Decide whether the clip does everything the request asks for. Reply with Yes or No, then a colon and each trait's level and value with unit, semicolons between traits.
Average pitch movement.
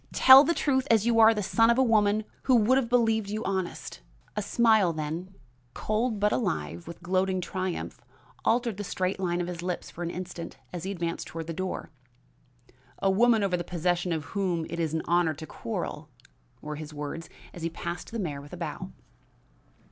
Yes: average, 4.5 semitones